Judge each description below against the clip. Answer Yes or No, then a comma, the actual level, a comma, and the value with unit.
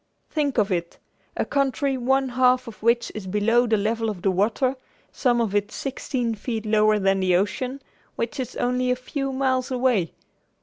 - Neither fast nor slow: Yes, average, 180 wpm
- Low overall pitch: No, high, 240 Hz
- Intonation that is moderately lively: Yes, average, 3.6 semitones